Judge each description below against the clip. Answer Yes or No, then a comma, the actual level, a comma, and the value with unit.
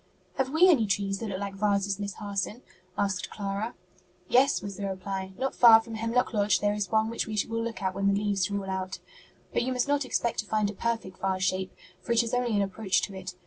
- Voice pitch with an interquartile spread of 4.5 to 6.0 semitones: No, average, 2.8 semitones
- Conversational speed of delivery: No, fast, 245 wpm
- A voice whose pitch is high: Yes, high, 205 Hz